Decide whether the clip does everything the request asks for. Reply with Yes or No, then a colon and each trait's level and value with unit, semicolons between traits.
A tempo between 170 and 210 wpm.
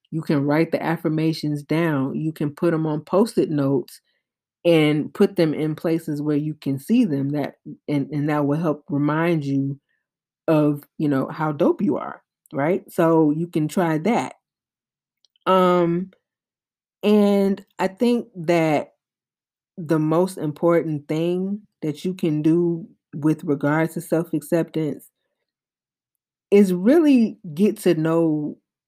No: average, 140 wpm